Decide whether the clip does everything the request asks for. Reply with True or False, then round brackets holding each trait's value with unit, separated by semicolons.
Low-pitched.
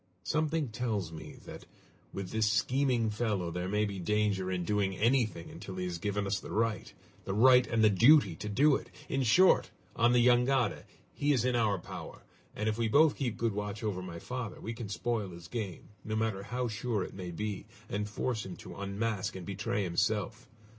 True (105 Hz)